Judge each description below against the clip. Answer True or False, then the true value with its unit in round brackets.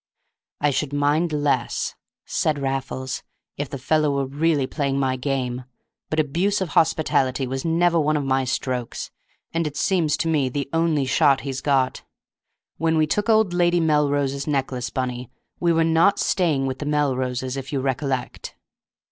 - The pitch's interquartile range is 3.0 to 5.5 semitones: True (3.3 semitones)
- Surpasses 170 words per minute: False (165 wpm)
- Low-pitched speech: False (145 Hz)